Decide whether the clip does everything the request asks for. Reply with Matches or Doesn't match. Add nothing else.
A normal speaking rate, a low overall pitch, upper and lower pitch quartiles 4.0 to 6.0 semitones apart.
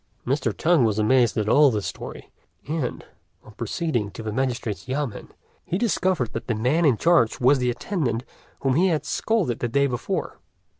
Matches